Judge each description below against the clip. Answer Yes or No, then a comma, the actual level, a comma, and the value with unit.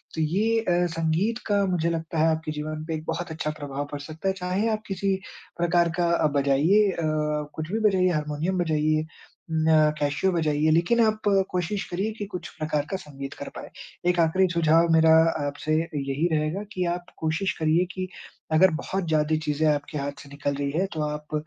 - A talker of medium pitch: Yes, medium, 160 Hz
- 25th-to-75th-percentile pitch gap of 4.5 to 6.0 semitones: No, average, 3.2 semitones